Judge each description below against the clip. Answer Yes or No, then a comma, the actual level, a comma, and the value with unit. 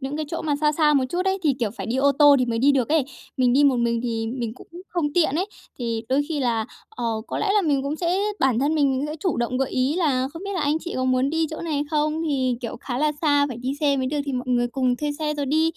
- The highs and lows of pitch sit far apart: No, average, 3.3 semitones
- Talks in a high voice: Yes, very high, 280 Hz